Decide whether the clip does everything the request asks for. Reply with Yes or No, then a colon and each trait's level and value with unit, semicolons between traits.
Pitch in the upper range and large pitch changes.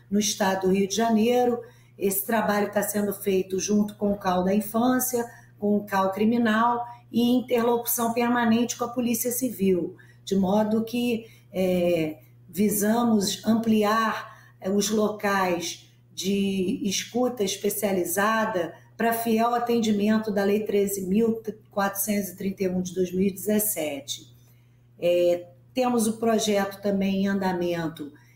No: high, 205 Hz; average, 3.4 semitones